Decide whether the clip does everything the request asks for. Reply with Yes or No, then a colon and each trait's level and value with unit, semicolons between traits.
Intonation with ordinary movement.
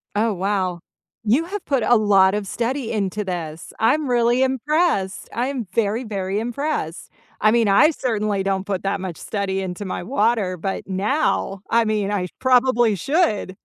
Yes: average, 4.2 semitones